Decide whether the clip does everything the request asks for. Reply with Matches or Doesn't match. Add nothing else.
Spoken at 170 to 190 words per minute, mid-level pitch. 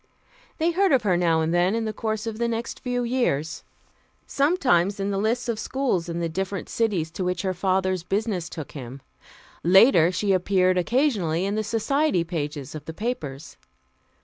Doesn't match